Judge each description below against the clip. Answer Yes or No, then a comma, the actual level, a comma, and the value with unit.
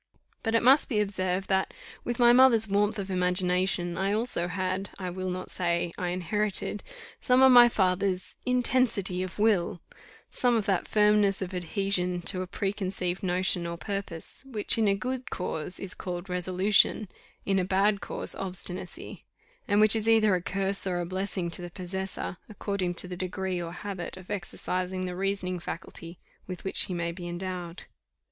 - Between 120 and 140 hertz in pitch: No, high, 190 Hz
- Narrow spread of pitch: Yes, narrow, 2.3 semitones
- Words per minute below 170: No, average, 175 wpm